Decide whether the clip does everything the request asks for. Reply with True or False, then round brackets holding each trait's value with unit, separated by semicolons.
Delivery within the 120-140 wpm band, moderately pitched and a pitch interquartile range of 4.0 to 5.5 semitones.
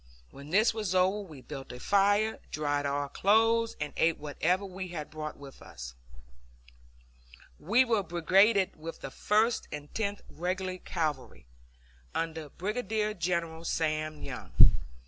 True (135 wpm; 175 Hz; 5.1 semitones)